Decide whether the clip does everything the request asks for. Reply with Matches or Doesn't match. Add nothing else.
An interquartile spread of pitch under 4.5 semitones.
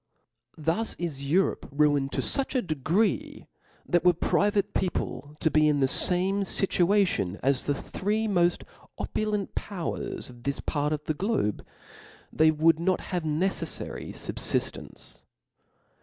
Doesn't match